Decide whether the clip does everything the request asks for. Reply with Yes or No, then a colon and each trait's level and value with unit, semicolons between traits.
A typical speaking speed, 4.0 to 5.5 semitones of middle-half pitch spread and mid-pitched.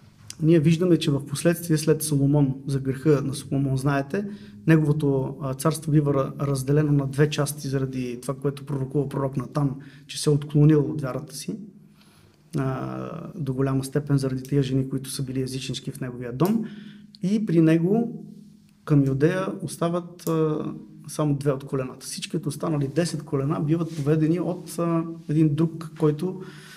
No: average, 145 wpm; average, 3.3 semitones; medium, 150 Hz